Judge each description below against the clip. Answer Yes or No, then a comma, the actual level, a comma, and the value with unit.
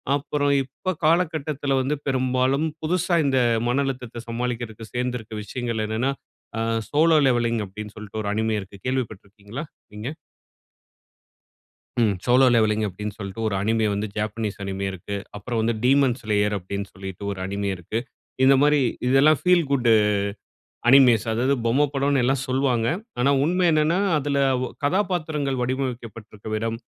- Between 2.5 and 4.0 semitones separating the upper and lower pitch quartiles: No, average, 4.4 semitones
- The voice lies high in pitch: No, low, 125 Hz